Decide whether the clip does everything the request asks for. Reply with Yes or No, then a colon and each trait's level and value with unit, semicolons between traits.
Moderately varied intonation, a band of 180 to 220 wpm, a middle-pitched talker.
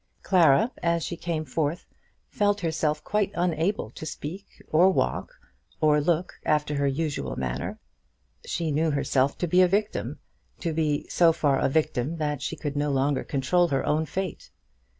No: average, 3.3 semitones; average, 165 wpm; medium, 155 Hz